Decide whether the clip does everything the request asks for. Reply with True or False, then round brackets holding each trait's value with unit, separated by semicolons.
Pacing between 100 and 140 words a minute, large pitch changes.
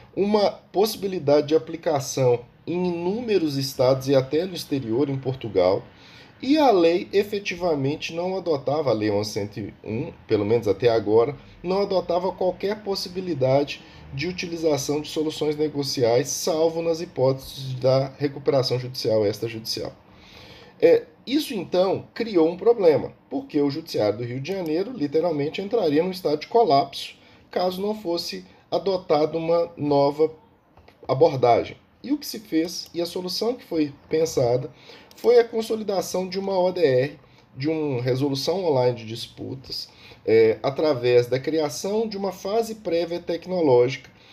True (135 wpm; 5.7 semitones)